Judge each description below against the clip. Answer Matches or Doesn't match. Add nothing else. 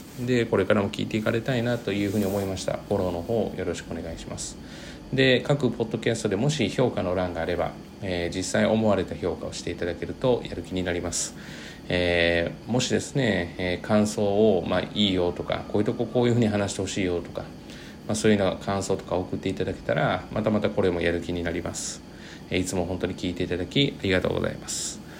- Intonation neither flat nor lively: Matches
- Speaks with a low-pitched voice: Matches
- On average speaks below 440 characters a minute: Doesn't match